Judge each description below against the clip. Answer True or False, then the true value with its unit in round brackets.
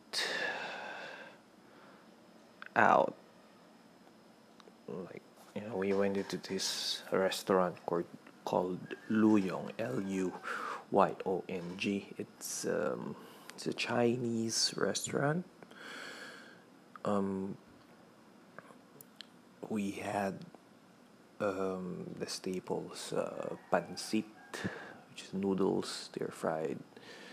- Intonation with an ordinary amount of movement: False (2.2 semitones)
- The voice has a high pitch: False (100 Hz)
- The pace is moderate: False (70 wpm)